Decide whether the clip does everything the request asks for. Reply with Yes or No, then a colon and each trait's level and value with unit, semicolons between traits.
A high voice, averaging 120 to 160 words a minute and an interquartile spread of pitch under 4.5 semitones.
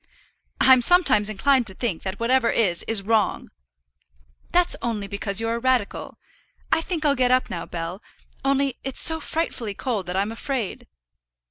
No: high, 230 Hz; average, 155 wpm; average, 5.1 semitones